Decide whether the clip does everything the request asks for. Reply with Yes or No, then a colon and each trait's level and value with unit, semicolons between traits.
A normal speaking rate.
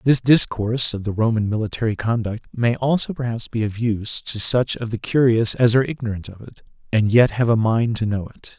No: fast, 215 wpm